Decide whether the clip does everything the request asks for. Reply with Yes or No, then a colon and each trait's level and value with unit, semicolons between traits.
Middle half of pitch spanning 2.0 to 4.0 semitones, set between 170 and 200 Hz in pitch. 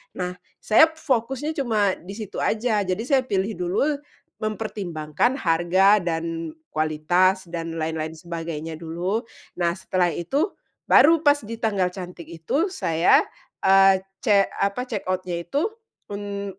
No: average, 4.7 semitones; high, 190 Hz